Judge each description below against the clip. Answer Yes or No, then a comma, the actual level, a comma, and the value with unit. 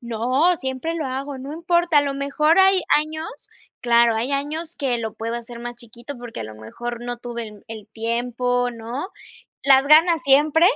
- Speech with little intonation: No, average, 4.4 semitones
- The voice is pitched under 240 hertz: No, very high, 260 Hz